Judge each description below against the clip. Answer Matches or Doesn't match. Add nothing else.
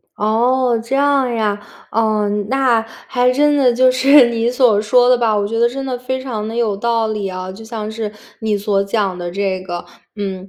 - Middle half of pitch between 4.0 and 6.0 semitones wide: Doesn't match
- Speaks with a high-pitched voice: Matches